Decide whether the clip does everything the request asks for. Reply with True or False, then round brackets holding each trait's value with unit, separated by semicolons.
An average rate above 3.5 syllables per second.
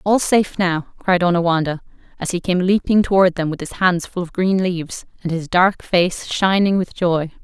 True (5.0 syllables/s)